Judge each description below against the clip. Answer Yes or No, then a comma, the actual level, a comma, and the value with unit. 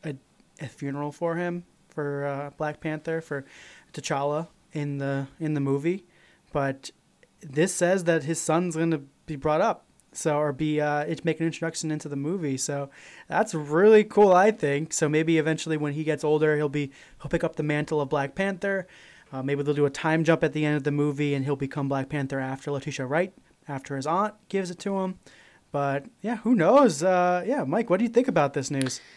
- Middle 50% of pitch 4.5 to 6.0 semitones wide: No, average, 3.2 semitones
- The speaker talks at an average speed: No, fast, 210 wpm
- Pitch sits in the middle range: Yes, medium, 155 Hz